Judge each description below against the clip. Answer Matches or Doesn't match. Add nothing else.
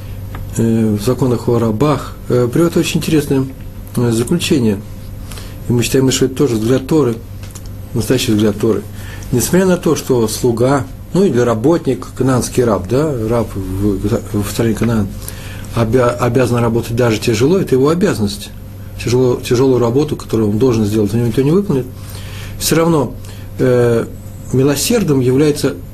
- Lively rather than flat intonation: Doesn't match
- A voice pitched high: Doesn't match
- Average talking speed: Matches